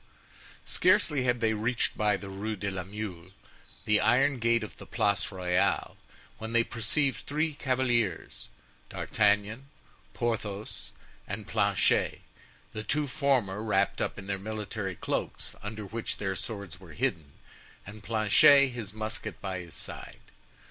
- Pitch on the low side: Yes, low, 110 Hz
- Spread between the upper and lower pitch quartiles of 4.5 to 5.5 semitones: No, average, 3.3 semitones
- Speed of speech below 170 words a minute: Yes, average, 140 wpm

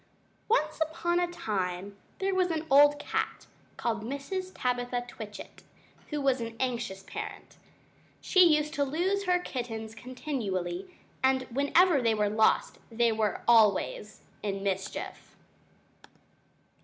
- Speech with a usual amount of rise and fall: No, wide, 6.4 semitones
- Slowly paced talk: Yes, slow, 130 wpm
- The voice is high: Yes, very high, 250 Hz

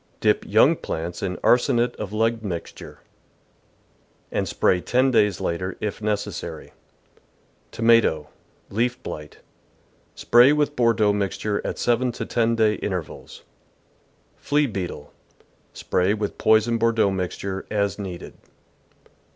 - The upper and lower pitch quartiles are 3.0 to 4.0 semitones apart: Yes, average, 3.6 semitones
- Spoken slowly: Yes, slow, 125 wpm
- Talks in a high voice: No, low, 105 Hz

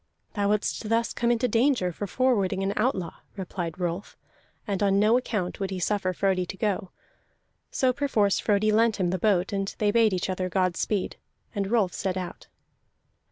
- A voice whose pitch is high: Yes, high, 200 Hz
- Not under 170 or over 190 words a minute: Yes, average, 180 wpm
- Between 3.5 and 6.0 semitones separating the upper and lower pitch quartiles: No, average, 2.9 semitones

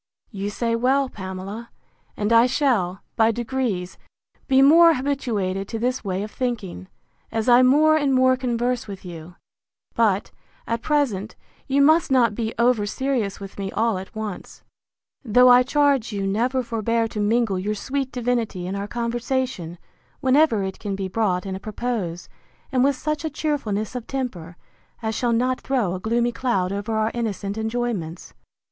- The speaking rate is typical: Yes, average, 165 wpm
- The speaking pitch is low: No, high, 230 Hz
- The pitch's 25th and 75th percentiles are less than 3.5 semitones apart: No, average, 4.3 semitones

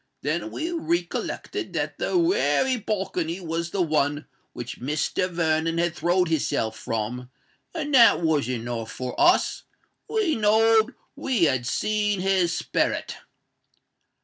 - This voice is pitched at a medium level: Yes, medium, 175 Hz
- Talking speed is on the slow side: Yes, slow, 130 wpm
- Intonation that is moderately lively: No, wide, 6.8 semitones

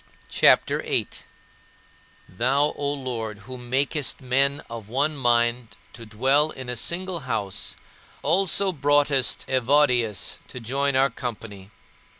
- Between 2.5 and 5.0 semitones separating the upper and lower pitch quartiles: Yes, average, 3.4 semitones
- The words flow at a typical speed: No, slow, 125 wpm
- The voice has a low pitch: Yes, low, 130 Hz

